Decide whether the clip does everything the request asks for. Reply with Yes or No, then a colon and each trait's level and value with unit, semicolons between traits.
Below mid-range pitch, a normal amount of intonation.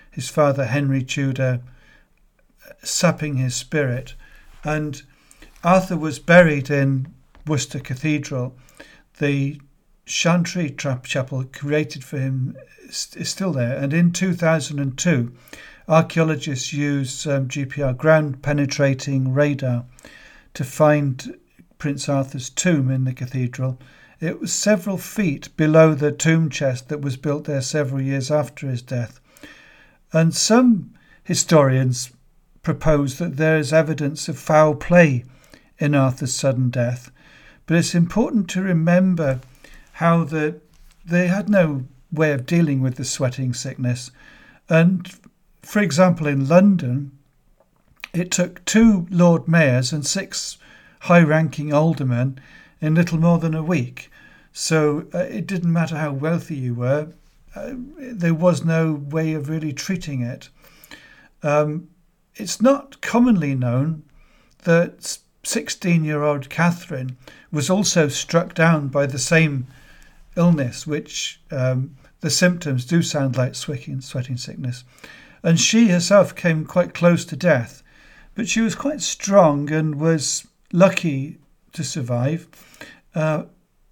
No: medium, 150 Hz; average, 3.9 semitones